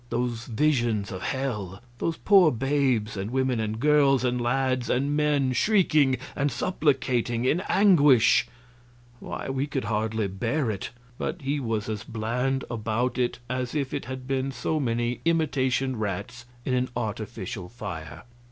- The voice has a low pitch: Yes, low, 125 Hz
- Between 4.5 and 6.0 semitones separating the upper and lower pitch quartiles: No, average, 3.5 semitones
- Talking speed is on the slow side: No, average, 150 wpm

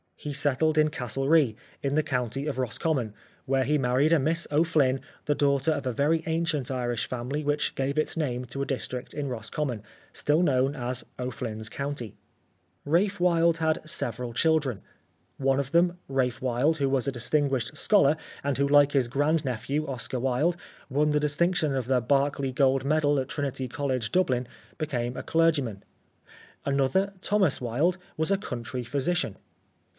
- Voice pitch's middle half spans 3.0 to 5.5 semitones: Yes, average, 3.3 semitones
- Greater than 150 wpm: Yes, average, 165 wpm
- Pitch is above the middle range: No, medium, 140 Hz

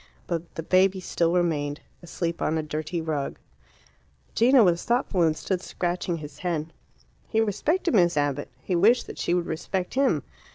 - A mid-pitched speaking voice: Yes, medium, 175 Hz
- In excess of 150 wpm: Yes, average, 165 wpm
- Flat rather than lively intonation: No, average, 3.1 semitones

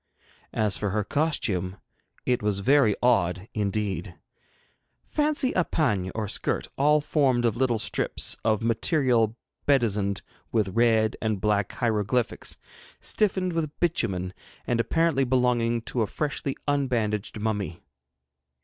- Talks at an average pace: No, slow, 120 wpm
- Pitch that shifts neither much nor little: Yes, average, 4.7 semitones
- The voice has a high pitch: No, low, 115 Hz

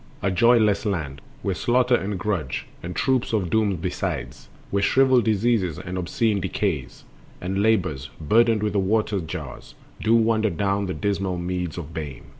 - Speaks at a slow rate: No, average, 160 wpm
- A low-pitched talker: Yes, low, 100 Hz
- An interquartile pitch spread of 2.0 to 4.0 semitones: Yes, average, 3.7 semitones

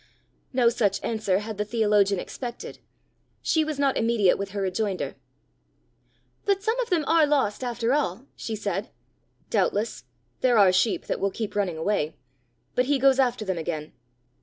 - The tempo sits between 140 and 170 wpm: Yes, average, 160 wpm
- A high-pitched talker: Yes, high, 220 Hz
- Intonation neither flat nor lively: Yes, average, 4.7 semitones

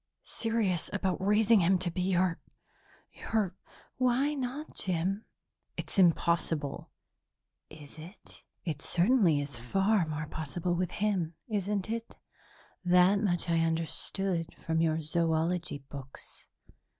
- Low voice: No, medium, 180 Hz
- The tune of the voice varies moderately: Yes, average, 3.9 semitones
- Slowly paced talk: Yes, slow, 120 wpm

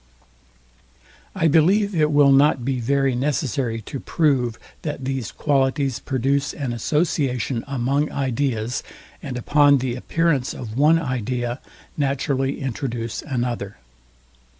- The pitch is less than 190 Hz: Yes, low, 135 Hz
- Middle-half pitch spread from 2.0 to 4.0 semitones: Yes, average, 2.9 semitones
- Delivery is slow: Yes, slow, 115 wpm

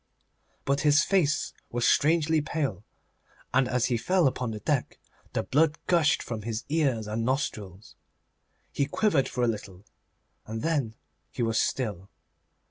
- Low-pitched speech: Yes, low, 130 Hz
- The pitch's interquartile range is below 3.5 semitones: No, average, 5.3 semitones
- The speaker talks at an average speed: Yes, average, 145 wpm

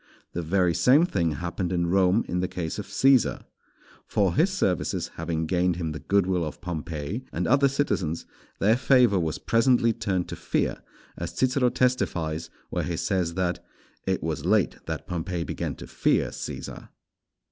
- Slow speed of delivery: No, average, 170 wpm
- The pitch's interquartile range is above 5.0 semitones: Yes, wide, 5.4 semitones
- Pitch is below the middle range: Yes, very low, 90 Hz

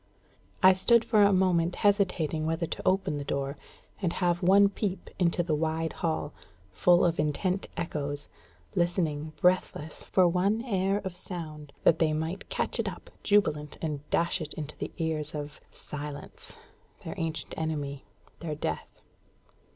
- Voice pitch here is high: No, medium, 165 Hz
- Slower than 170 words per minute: Yes, average, 150 wpm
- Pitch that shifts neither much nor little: Yes, average, 3.5 semitones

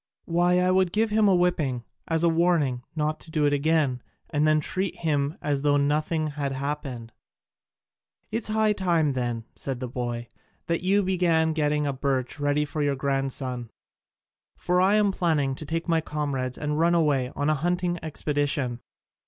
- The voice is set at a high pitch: No, medium, 150 Hz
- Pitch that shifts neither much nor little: Yes, average, 3.8 semitones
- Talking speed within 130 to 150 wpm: No, average, 175 wpm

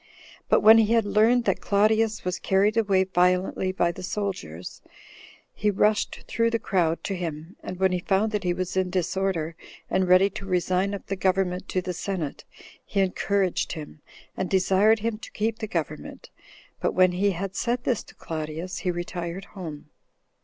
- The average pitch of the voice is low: No, high, 190 Hz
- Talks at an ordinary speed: Yes, average, 180 wpm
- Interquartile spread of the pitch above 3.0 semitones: No, narrow, 2.4 semitones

